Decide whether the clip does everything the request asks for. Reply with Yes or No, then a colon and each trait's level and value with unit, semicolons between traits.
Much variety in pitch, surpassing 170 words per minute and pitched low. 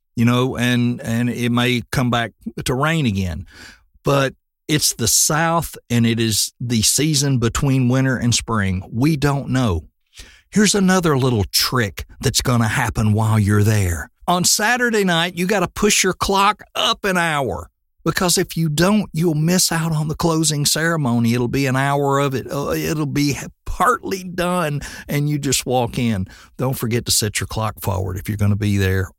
Yes: wide, 6.3 semitones; average, 185 wpm; low, 130 Hz